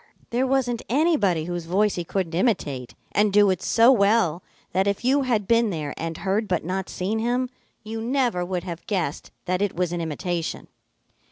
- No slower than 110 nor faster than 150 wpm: No, average, 185 wpm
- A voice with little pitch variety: No, average, 4.8 semitones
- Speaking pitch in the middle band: No, high, 195 Hz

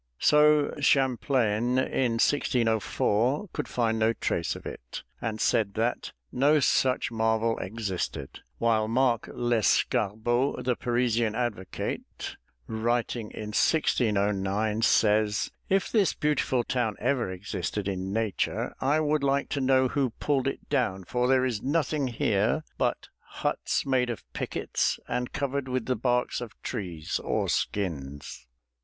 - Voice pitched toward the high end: No, low, 120 Hz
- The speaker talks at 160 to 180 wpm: No, slow, 135 wpm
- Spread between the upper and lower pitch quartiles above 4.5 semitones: No, average, 3.7 semitones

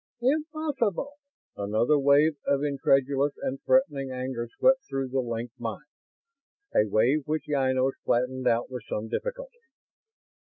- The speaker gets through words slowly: Yes, slow, 125 wpm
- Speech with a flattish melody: No, average, 3.8 semitones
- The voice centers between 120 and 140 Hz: Yes, low, 135 Hz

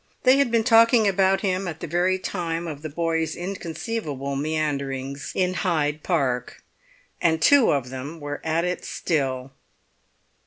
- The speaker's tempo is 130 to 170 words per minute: Yes, average, 150 wpm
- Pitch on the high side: No, medium, 165 Hz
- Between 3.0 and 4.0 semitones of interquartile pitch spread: No, average, 4.5 semitones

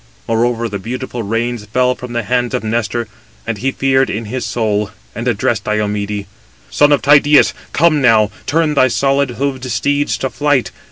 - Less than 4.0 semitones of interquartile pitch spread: Yes, average, 3.4 semitones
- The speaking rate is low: No, average, 170 wpm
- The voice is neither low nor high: No, low, 120 Hz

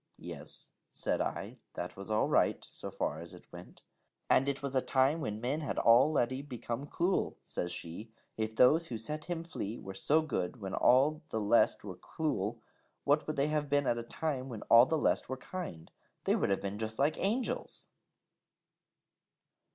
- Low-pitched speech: Yes, low, 130 Hz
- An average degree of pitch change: No, wide, 5.8 semitones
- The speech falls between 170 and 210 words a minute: Yes, average, 190 wpm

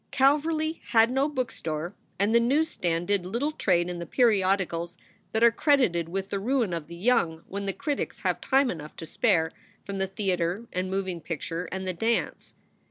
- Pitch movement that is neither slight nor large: No, wide, 5.9 semitones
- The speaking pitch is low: No, high, 195 Hz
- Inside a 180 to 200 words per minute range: Yes, average, 185 wpm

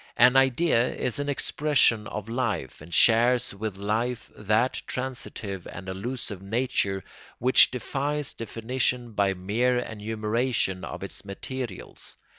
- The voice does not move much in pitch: No, average, 3.8 semitones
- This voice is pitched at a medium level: No, low, 115 Hz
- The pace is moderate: No, slow, 120 wpm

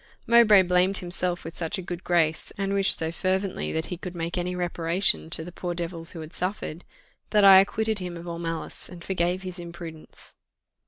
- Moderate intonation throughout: No, narrow, 2.0 semitones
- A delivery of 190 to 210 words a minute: Yes, average, 200 wpm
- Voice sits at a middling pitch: Yes, medium, 175 Hz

